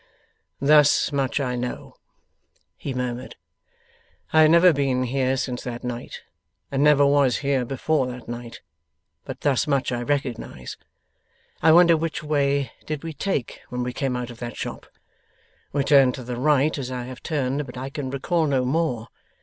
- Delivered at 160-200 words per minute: Yes, average, 170 wpm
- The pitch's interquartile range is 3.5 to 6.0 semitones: No, average, 2.8 semitones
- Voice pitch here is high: No, low, 135 Hz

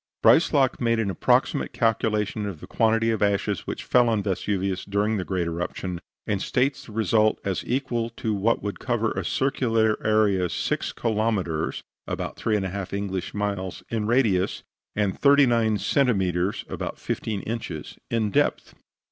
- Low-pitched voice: Yes, low, 105 Hz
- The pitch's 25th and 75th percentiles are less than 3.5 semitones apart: Yes, average, 2.9 semitones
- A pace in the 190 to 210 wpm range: No, average, 150 wpm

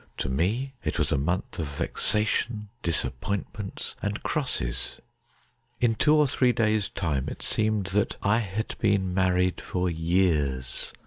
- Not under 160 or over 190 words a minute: No, average, 145 wpm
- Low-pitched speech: Yes, low, 100 Hz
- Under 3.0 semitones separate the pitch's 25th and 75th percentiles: No, average, 4.3 semitones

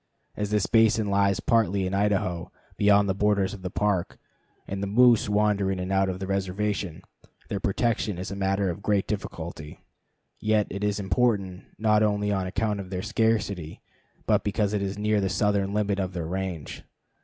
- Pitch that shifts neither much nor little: No, narrow, 1.6 semitones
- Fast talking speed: No, average, 185 wpm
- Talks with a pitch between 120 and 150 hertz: No, low, 100 Hz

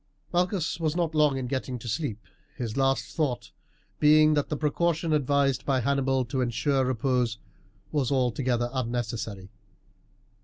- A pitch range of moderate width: Yes, average, 3.5 semitones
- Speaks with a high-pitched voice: No, low, 135 Hz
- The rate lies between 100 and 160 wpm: Yes, average, 140 wpm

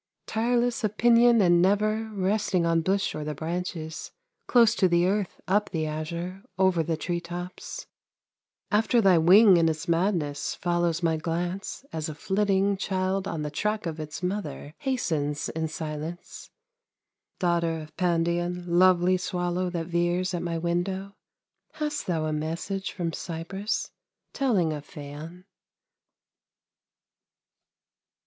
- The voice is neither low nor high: Yes, medium, 175 Hz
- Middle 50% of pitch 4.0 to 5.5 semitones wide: No, average, 3.1 semitones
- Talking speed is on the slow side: Yes, slow, 130 wpm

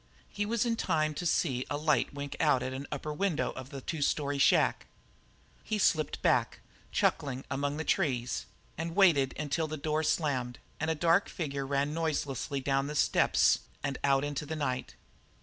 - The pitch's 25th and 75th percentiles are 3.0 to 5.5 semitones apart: No, narrow, 2.6 semitones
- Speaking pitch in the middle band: Yes, medium, 145 Hz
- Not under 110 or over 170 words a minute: No, average, 185 wpm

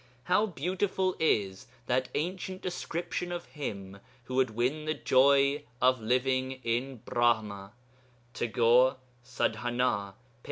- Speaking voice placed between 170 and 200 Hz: No, low, 130 Hz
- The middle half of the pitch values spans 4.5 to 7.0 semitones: Yes, average, 4.8 semitones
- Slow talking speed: Yes, slow, 115 wpm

